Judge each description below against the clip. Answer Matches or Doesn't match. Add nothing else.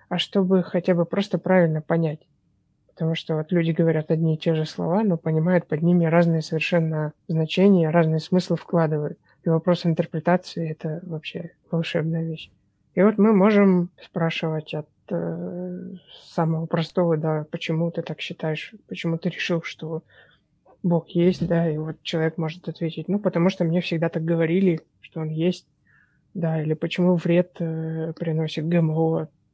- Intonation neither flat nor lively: Doesn't match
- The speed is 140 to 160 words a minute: Matches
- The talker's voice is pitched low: Doesn't match